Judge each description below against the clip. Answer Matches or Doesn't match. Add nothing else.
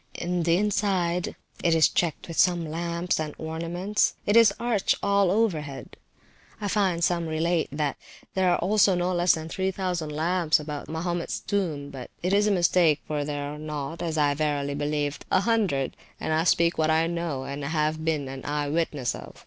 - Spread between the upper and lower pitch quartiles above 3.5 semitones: Doesn't match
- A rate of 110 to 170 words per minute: Doesn't match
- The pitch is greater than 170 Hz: Doesn't match